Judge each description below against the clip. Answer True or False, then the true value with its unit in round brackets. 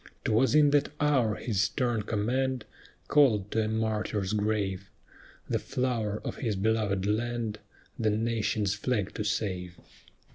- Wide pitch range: False (2.6 semitones)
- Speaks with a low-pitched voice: True (110 Hz)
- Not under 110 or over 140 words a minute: True (135 wpm)